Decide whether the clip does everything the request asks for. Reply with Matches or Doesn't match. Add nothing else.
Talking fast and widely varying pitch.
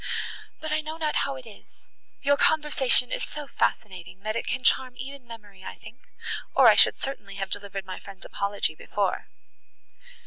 Doesn't match